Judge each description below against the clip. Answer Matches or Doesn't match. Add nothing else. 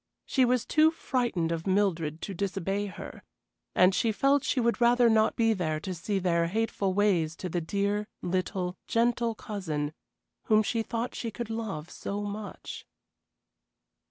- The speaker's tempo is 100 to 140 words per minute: Doesn't match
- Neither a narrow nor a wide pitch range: Matches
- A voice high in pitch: Matches